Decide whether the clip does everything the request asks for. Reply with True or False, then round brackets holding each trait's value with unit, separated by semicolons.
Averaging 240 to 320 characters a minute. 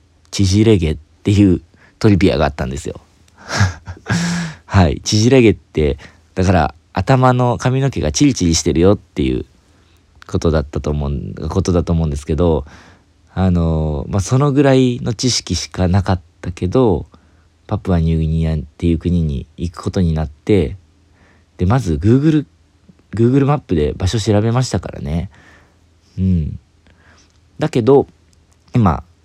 True (285 characters per minute)